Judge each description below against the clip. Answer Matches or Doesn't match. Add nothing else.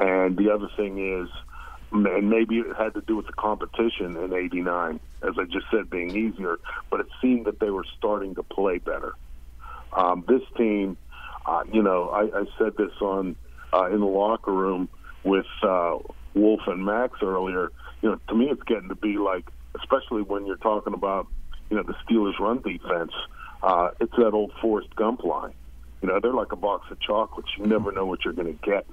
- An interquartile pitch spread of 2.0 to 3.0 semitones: Matches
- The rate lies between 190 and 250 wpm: Matches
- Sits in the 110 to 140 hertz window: Doesn't match